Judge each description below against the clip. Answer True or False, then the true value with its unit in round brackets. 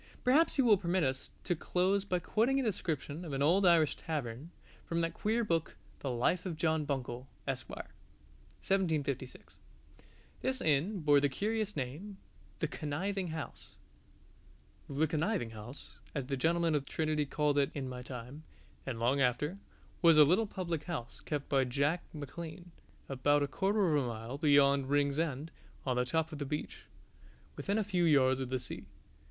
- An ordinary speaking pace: True (170 wpm)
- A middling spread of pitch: True (4.6 semitones)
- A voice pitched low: False (150 Hz)